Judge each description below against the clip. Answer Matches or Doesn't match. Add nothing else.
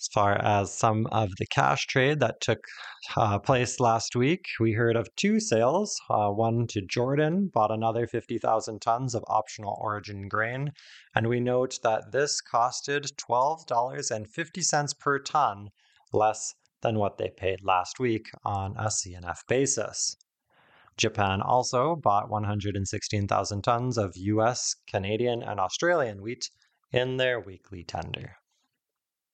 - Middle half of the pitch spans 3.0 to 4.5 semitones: Matches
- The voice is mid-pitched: Doesn't match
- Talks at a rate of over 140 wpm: Doesn't match